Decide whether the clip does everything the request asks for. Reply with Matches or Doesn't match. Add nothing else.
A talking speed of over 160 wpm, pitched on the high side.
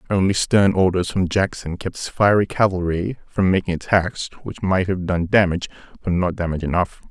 Doesn't match